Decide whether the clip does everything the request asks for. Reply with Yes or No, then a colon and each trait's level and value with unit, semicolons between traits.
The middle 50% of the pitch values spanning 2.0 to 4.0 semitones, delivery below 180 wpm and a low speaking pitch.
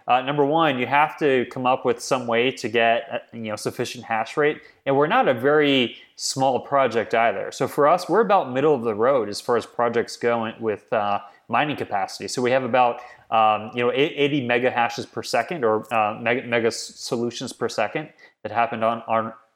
No: narrow, 2.5 semitones; fast, 205 wpm; low, 120 Hz